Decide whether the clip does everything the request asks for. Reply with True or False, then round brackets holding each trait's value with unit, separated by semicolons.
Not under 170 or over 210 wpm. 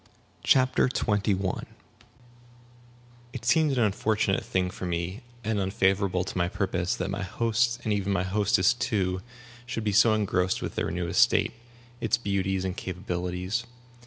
False (150 wpm)